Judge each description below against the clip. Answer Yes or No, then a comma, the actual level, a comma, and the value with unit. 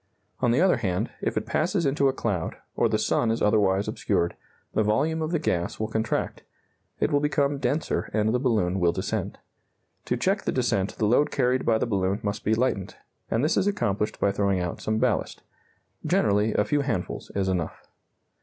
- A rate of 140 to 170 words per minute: No, average, 195 wpm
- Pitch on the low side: Yes, low, 110 Hz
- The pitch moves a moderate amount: No, wide, 5.7 semitones